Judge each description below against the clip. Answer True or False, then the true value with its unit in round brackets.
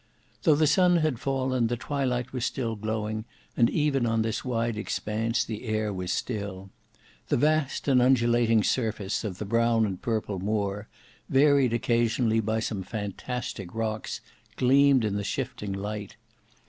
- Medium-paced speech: True (150 wpm)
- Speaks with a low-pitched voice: True (115 Hz)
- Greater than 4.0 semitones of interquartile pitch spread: False (3.1 semitones)